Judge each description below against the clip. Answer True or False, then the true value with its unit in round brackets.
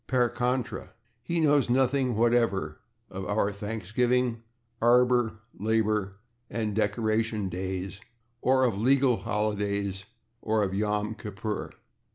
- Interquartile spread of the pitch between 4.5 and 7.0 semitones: False (3.2 semitones)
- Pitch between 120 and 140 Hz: False (110 Hz)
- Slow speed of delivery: True (110 wpm)